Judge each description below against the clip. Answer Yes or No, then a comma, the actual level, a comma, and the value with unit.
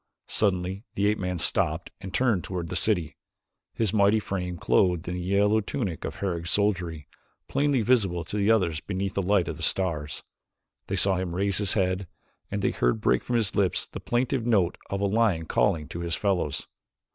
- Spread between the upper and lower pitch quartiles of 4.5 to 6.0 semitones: No, average, 2.9 semitones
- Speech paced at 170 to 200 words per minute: Yes, average, 190 wpm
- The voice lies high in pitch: No, very low, 95 Hz